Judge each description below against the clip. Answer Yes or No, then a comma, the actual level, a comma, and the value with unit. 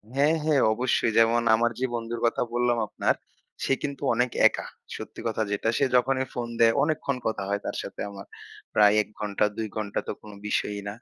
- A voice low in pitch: Yes, low, 115 Hz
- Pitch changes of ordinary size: Yes, average, 3.3 semitones